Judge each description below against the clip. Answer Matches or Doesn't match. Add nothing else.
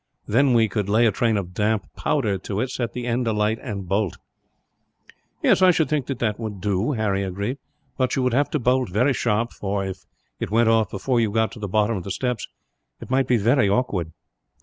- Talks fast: Matches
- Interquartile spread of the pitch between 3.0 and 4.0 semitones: Matches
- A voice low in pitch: Matches